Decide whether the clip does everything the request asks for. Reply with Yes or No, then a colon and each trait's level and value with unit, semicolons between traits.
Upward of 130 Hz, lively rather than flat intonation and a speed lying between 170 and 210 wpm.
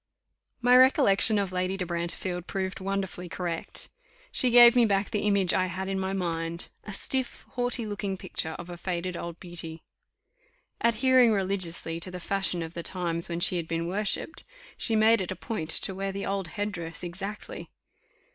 No: high, 190 Hz; average, 3.2 semitones; average, 180 wpm